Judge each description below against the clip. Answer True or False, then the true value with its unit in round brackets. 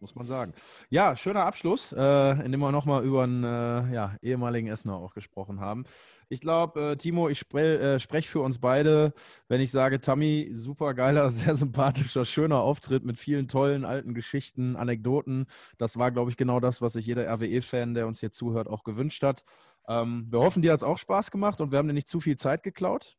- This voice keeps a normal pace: False (210 wpm)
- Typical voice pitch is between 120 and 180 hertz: True (130 Hz)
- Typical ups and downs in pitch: True (3.4 semitones)